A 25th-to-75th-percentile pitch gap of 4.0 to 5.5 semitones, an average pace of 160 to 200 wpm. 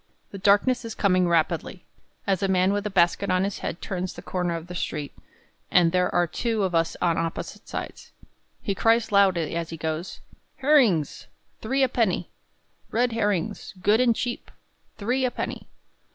Yes: average, 4.4 semitones; average, 175 wpm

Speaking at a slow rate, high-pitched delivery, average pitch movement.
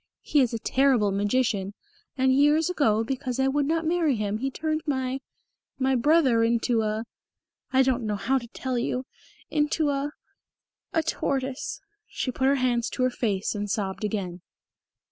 No: average, 165 wpm; very high, 255 Hz; average, 3.9 semitones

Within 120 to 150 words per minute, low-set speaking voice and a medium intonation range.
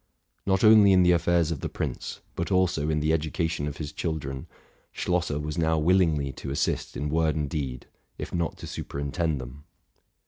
No: average, 185 wpm; very low, 80 Hz; average, 3.0 semitones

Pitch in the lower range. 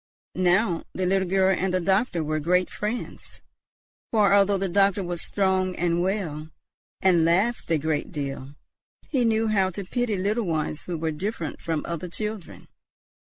No: medium, 185 Hz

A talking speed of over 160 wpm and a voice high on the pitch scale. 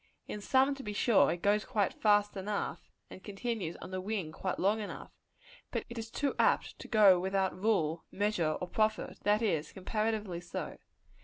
Yes: average, 180 wpm; high, 205 Hz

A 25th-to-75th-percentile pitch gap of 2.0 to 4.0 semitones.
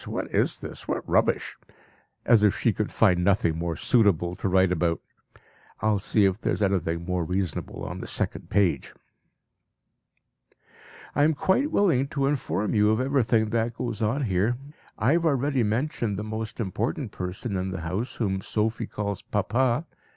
No: average, 4.4 semitones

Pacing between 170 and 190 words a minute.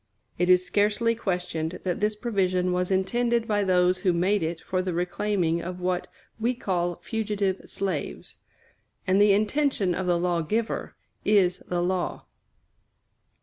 No: average, 150 wpm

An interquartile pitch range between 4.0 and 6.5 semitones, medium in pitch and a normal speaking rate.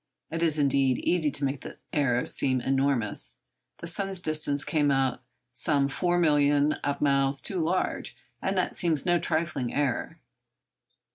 No: average, 3.3 semitones; medium, 145 Hz; average, 150 wpm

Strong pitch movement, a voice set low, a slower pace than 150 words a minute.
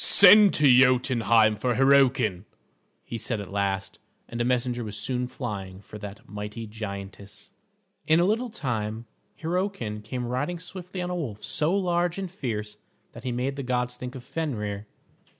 No: wide, 6.2 semitones; low, 125 Hz; average, 165 wpm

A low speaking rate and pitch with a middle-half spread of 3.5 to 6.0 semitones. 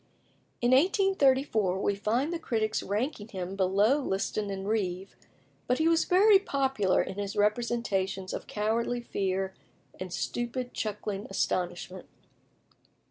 Yes: slow, 125 wpm; average, 5.0 semitones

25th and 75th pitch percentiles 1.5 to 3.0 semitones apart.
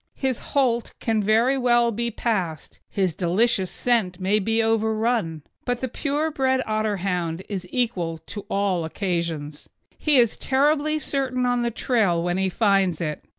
No: average, 5.2 semitones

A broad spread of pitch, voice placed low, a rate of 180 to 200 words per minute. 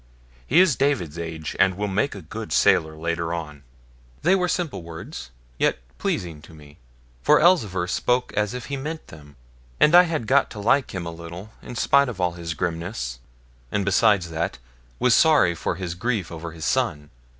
Yes: wide, 7.2 semitones; very low, 95 Hz; average, 185 wpm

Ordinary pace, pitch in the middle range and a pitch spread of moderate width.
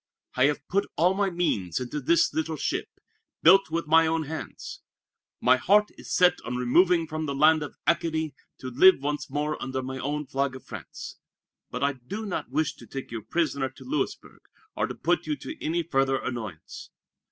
Yes: average, 195 wpm; medium, 150 Hz; average, 4.2 semitones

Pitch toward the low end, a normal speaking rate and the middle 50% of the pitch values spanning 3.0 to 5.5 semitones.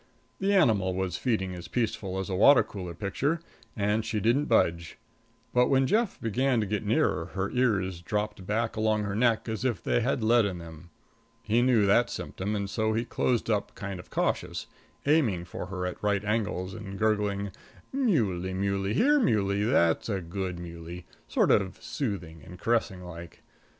Yes: low, 105 Hz; average, 175 wpm; average, 3.8 semitones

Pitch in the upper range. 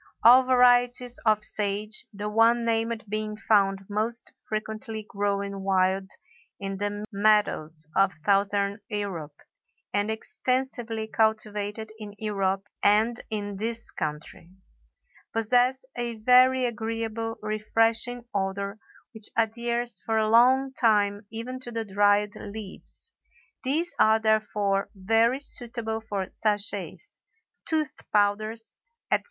Yes: high, 215 Hz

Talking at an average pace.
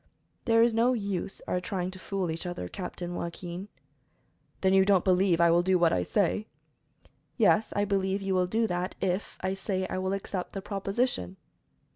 Yes: average, 190 wpm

